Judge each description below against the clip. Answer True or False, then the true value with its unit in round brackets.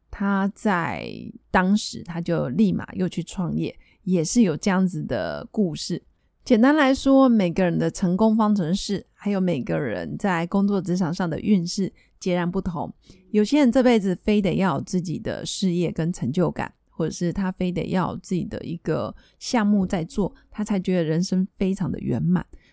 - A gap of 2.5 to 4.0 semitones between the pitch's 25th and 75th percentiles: True (3.0 semitones)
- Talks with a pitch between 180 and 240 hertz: True (190 Hz)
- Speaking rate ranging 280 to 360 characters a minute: False (260 characters per minute)